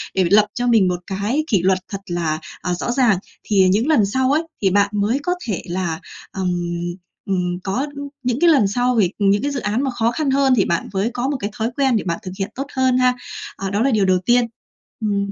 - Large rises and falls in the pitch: No, average, 4.9 semitones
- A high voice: Yes, high, 205 Hz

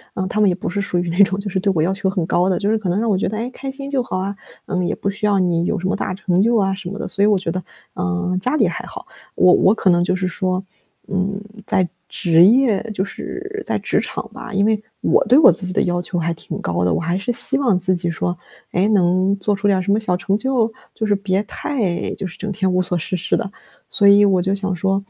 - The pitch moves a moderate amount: No, narrow, 2.3 semitones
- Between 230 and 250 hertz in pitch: No, high, 195 Hz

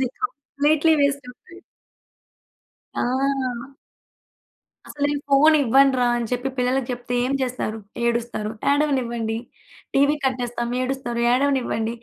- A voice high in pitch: Yes, very high, 260 Hz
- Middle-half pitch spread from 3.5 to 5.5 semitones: No, average, 2.8 semitones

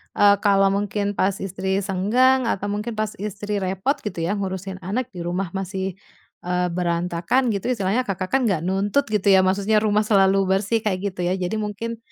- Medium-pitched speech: No, high, 195 Hz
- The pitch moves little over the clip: Yes, narrow, 2.1 semitones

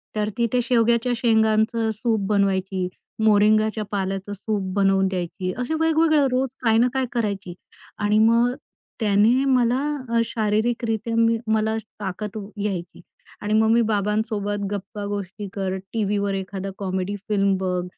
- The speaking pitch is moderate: No, high, 215 Hz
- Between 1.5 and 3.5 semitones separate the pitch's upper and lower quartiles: Yes, narrow, 2.6 semitones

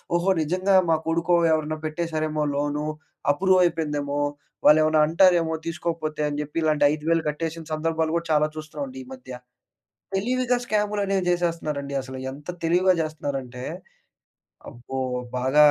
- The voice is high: No, medium, 160 Hz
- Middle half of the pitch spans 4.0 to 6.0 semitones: No, average, 2.7 semitones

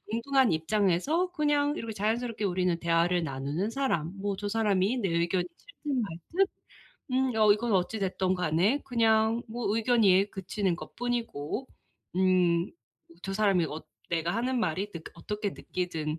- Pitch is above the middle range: Yes, high, 200 Hz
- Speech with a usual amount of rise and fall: Yes, average, 5.0 semitones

